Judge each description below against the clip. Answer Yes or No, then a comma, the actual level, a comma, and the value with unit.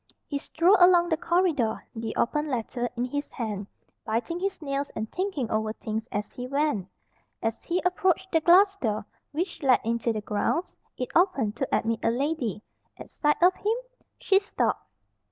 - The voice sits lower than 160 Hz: No, very high, 280 Hz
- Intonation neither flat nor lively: No, wide, 7.6 semitones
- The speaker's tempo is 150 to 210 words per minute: Yes, average, 170 wpm